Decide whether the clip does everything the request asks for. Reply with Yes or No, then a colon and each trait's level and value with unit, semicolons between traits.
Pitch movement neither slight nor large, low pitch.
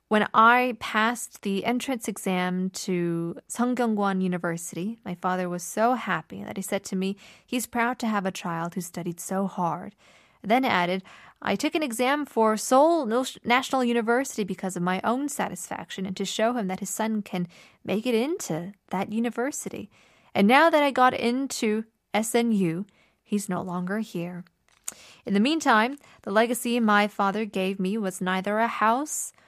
No: average, 4.1 semitones; high, 210 Hz